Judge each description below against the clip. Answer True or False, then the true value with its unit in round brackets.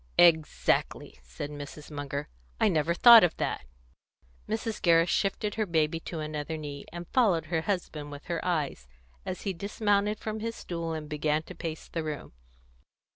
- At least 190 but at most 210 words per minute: False (165 wpm)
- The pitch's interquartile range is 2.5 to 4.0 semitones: False (4.5 semitones)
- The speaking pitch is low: False (165 Hz)